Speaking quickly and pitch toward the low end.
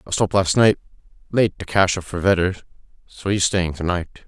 Yes: fast, 210 wpm; very low, 90 Hz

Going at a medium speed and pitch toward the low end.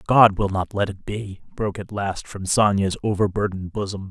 Yes: average, 190 wpm; low, 100 Hz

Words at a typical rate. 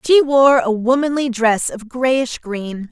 Yes: average, 165 wpm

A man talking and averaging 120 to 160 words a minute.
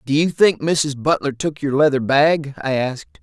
No: male; fast, 205 wpm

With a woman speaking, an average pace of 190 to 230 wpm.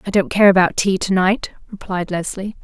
Yes: female; fast, 205 wpm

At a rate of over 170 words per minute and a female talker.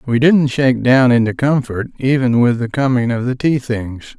No: average, 200 wpm; male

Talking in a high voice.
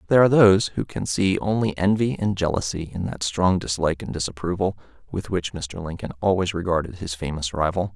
No: very low, 90 Hz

